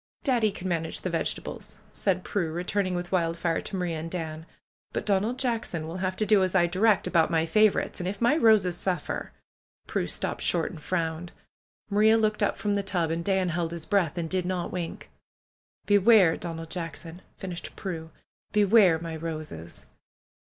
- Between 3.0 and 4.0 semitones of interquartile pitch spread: Yes, average, 3.3 semitones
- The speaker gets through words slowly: No, average, 185 wpm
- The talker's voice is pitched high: No, medium, 180 Hz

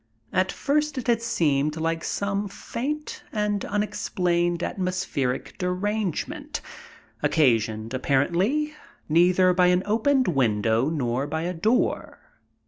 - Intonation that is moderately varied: No, wide, 5.9 semitones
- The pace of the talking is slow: Yes, slow, 110 wpm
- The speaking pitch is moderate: Yes, medium, 180 Hz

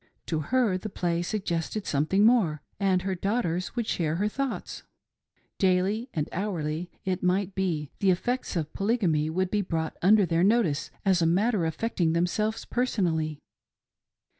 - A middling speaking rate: Yes, average, 150 wpm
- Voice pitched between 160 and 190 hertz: Yes, medium, 185 Hz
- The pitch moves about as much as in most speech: Yes, average, 4.2 semitones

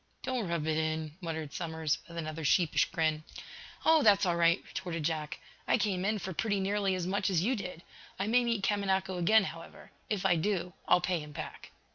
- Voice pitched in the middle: Yes, medium, 180 Hz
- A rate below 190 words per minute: No, average, 200 wpm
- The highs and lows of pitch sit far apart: No, average, 3.8 semitones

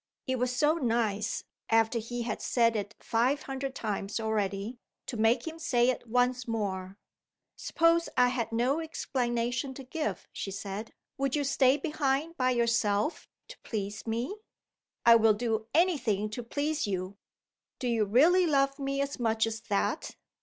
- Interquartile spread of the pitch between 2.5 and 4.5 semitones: Yes, average, 3.8 semitones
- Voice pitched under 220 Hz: No, high, 240 Hz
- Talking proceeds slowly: No, average, 160 wpm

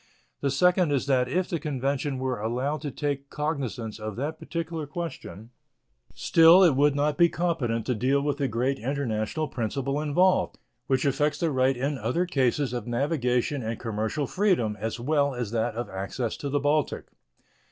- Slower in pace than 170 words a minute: No, average, 175 wpm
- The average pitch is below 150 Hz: Yes, medium, 140 Hz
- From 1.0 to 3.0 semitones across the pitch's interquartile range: No, average, 3.7 semitones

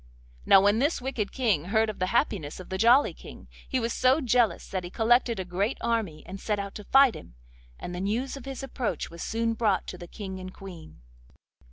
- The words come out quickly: Yes, fast, 220 wpm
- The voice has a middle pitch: No, high, 215 Hz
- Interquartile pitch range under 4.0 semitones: No, average, 4.3 semitones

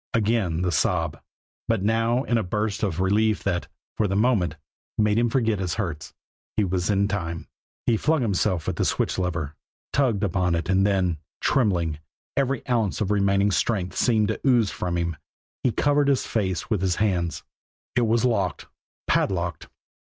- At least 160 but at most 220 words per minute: Yes, average, 170 wpm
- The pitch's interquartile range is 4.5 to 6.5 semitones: No, average, 4.0 semitones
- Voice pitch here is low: Yes, low, 100 Hz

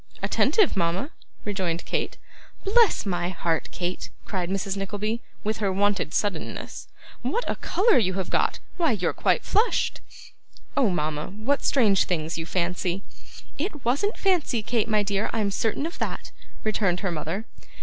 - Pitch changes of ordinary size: Yes, average, 5.0 semitones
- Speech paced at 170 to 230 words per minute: No, average, 150 wpm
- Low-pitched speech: No, high, 200 Hz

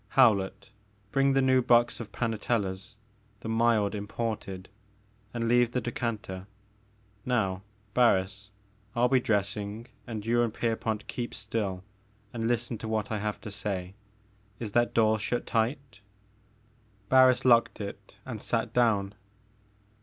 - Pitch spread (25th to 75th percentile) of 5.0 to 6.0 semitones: No, narrow, 2.6 semitones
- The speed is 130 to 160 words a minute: Yes, average, 145 wpm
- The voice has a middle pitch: No, low, 110 Hz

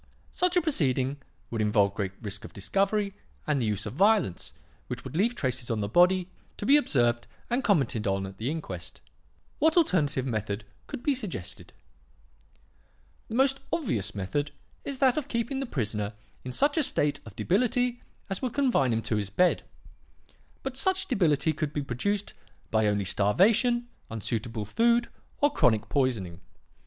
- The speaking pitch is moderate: Yes, medium, 145 Hz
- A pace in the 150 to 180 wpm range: Yes, average, 165 wpm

